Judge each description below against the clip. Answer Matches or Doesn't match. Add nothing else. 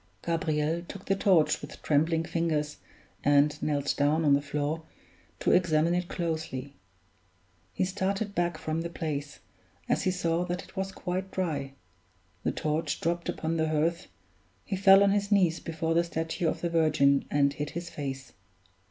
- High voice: Doesn't match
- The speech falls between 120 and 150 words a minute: Doesn't match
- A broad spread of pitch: Doesn't match